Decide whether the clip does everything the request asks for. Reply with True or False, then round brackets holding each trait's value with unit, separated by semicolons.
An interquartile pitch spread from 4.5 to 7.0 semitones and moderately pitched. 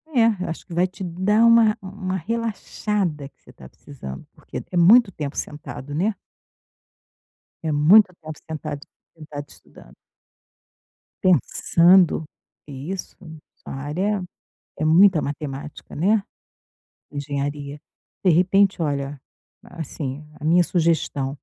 True (4.9 semitones; 165 Hz)